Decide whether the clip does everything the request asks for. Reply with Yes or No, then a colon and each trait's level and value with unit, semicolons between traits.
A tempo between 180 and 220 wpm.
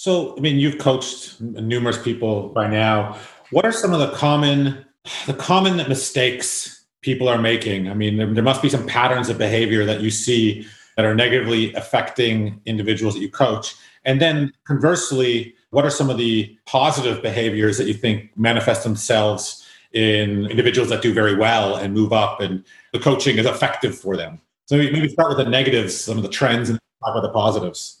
Yes: average, 190 wpm